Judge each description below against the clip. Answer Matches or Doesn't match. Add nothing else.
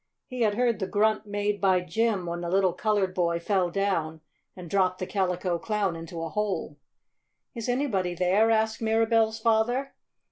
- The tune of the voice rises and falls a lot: Doesn't match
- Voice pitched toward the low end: Doesn't match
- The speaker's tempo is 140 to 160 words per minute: Doesn't match